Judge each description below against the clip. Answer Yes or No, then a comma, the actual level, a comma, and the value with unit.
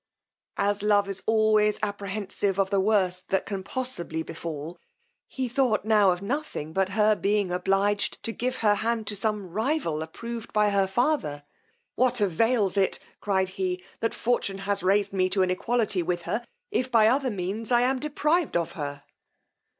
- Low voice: No, high, 205 Hz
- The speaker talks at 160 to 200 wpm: Yes, average, 170 wpm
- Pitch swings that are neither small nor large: Yes, average, 3.2 semitones